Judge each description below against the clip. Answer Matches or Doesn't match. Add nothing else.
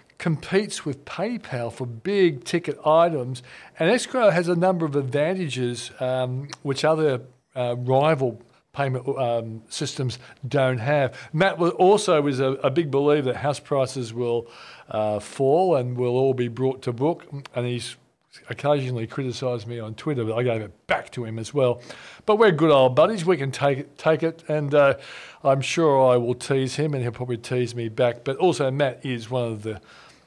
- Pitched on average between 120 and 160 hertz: Matches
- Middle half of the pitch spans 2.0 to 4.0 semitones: Matches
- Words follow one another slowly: Doesn't match